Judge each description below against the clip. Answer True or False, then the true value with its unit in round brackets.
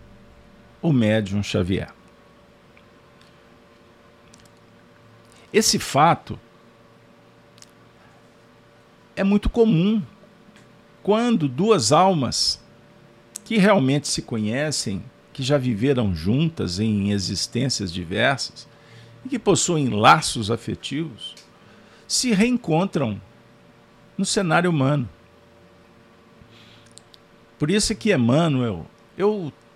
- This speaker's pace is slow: True (80 wpm)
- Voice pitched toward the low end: True (115 Hz)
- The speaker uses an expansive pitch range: True (6.0 semitones)